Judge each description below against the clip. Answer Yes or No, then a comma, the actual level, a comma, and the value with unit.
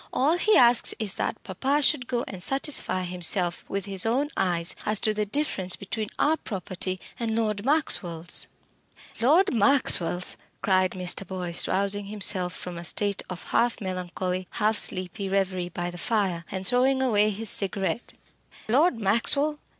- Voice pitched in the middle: No, high, 200 Hz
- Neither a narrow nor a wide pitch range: Yes, average, 4.6 semitones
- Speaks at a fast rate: No, average, 160 wpm